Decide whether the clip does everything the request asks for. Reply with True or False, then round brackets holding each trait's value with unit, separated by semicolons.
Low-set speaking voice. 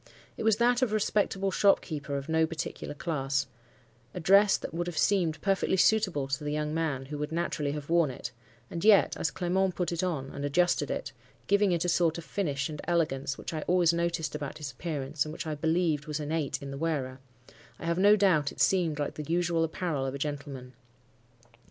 False (160 Hz)